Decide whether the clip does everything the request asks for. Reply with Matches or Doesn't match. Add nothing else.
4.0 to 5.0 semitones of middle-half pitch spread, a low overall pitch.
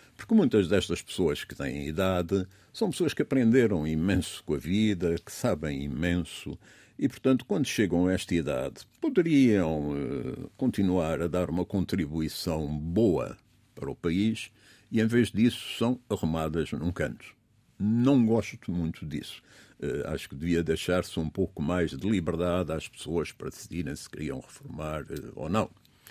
Matches